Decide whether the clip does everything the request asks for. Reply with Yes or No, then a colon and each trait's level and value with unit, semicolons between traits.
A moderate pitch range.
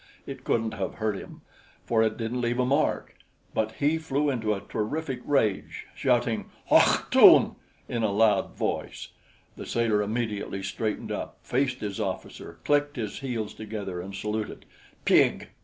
Yes: average, 3.3 semitones